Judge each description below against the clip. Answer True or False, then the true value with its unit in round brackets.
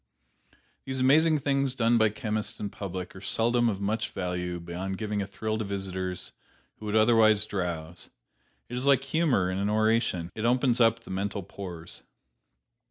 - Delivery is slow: False (165 wpm)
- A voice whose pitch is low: True (105 Hz)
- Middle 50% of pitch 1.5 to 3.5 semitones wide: False (4.0 semitones)